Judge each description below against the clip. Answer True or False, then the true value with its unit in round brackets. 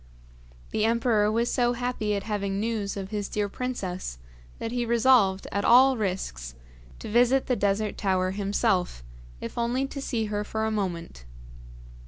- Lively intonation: False (3.3 semitones)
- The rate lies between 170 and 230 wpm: False (160 wpm)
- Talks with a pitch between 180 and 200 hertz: False (210 Hz)